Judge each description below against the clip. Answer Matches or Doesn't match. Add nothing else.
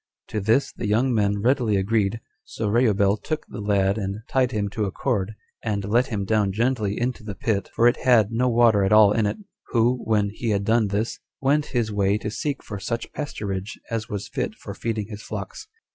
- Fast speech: Matches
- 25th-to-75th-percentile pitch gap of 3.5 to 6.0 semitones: Doesn't match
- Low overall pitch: Matches